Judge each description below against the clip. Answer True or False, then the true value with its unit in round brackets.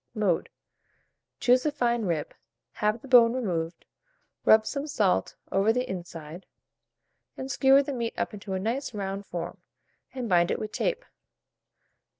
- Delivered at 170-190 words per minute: False (150 wpm)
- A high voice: True (220 Hz)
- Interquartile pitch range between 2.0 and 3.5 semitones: False (5.1 semitones)